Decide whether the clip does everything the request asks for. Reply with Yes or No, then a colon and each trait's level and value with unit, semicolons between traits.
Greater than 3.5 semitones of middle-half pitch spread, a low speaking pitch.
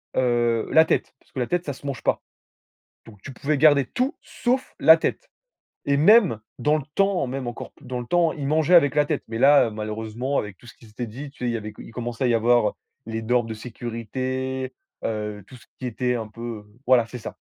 Yes: average, 4.0 semitones; low, 125 Hz